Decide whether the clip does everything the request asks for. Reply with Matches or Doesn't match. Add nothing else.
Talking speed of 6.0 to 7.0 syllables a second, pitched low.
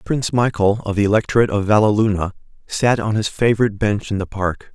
Matches